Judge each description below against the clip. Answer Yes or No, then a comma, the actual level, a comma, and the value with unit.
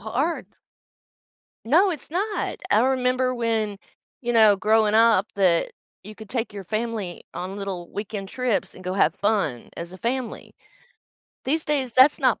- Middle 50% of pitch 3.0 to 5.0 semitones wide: Yes, average, 4.2 semitones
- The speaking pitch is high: Yes, high, 225 Hz